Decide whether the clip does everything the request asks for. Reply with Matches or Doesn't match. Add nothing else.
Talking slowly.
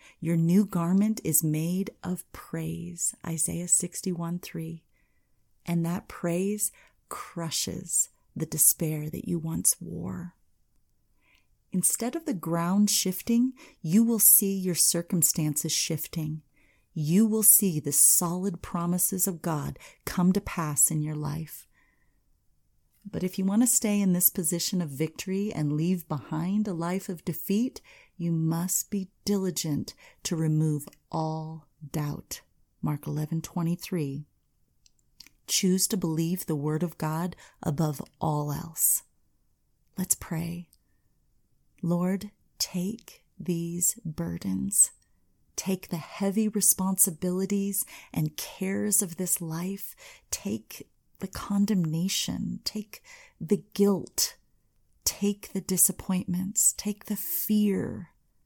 Matches